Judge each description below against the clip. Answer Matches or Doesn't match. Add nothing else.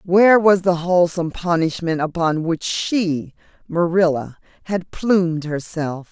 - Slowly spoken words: Matches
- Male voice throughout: Doesn't match